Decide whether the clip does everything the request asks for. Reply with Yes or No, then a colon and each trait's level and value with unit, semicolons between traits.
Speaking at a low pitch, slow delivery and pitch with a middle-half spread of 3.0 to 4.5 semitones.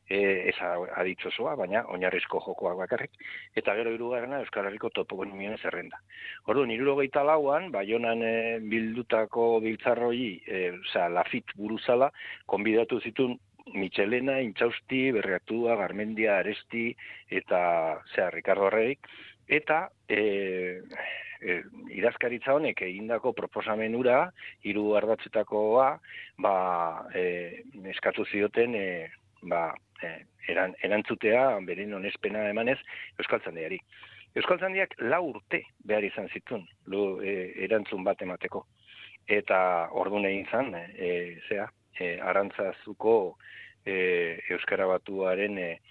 Yes: low, 110 Hz; slow, 105 wpm; average, 3.7 semitones